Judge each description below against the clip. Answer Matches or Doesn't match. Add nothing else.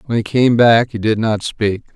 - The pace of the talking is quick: Matches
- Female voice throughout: Doesn't match